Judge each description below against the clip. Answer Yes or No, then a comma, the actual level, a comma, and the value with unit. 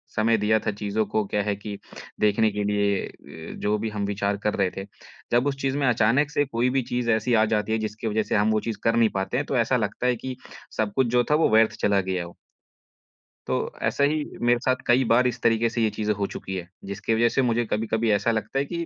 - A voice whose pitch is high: No, low, 110 Hz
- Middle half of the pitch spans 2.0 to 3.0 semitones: Yes, average, 2.7 semitones